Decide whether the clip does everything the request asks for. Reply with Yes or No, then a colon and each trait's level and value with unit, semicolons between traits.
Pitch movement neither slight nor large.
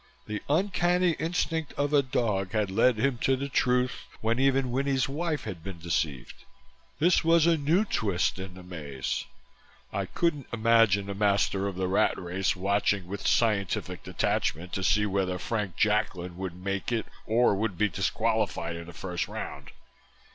No: wide, 6.0 semitones